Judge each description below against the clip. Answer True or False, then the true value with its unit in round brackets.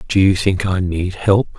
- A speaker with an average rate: False (225 wpm)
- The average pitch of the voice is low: True (95 Hz)